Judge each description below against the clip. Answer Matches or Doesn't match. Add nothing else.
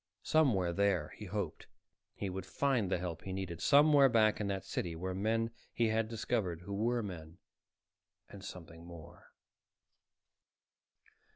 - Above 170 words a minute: Doesn't match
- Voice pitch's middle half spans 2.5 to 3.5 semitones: Doesn't match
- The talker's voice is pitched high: Doesn't match